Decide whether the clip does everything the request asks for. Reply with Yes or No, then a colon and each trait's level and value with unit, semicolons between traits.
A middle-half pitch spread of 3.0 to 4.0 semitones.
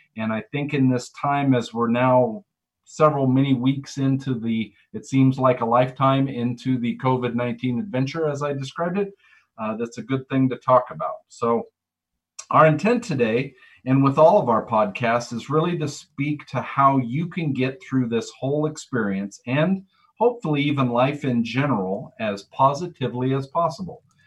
Yes: average, 3.6 semitones